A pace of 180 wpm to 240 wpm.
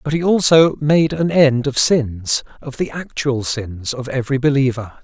No: average, 165 wpm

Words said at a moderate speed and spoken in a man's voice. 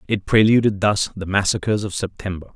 Yes: average, 165 wpm; male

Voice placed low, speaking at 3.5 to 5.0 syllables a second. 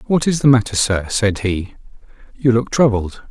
Yes: low, 115 Hz; 4.7 syllables/s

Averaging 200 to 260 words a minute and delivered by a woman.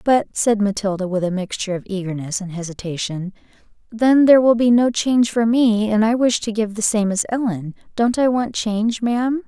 Yes: fast, 205 wpm; female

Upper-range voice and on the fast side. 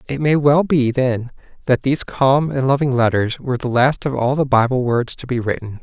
No: low, 130 Hz; fast, 225 wpm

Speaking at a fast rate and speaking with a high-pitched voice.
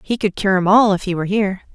Yes: fast, 310 wpm; high, 195 Hz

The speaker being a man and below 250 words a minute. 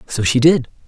Yes: male; fast, 205 wpm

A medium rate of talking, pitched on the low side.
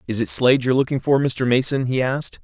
No: fast, 245 wpm; low, 125 Hz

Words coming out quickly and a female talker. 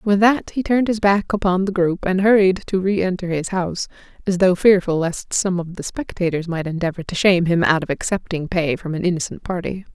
Yes: fast, 215 wpm; female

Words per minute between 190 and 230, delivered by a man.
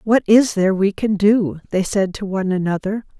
No: fast, 205 wpm; female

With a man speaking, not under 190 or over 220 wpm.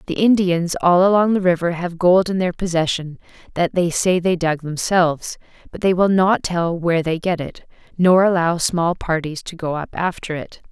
No: female; average, 195 wpm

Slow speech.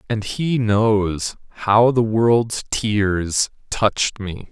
Yes: slow, 120 wpm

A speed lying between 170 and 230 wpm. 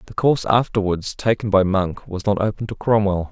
Yes: average, 200 wpm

